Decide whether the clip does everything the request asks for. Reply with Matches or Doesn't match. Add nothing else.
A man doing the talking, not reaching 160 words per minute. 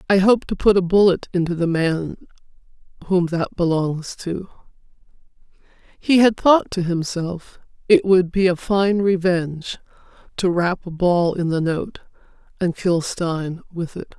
Doesn't match